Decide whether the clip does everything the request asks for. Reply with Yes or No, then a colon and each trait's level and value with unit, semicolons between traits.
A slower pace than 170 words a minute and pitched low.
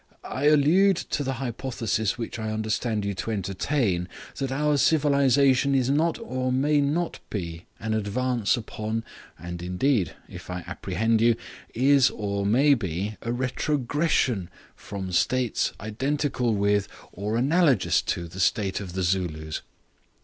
Yes: average, 140 wpm; low, 115 Hz